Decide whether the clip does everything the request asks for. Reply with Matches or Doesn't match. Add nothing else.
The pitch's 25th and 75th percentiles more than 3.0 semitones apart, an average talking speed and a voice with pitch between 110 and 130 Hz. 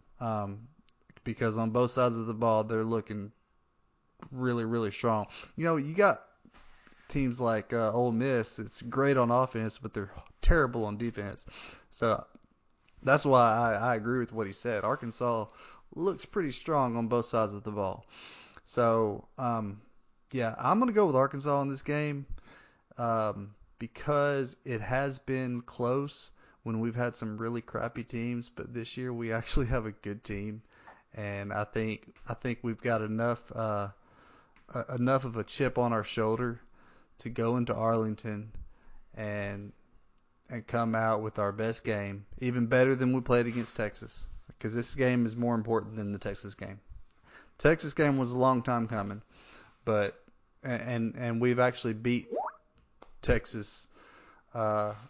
Doesn't match